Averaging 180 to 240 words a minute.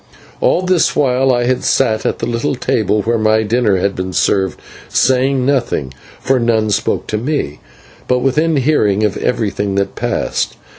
No: average, 160 wpm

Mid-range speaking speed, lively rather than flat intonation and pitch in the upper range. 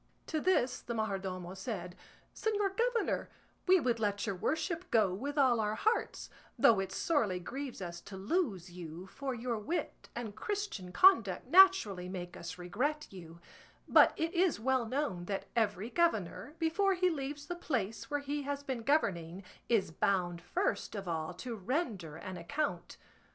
Yes: average, 160 wpm; wide, 8.4 semitones; high, 230 Hz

